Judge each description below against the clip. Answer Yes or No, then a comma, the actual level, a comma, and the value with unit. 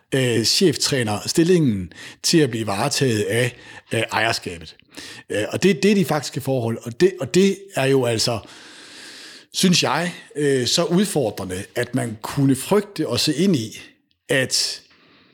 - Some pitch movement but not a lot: No, wide, 6.3 semitones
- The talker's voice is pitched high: No, low, 135 Hz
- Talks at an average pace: No, slow, 135 wpm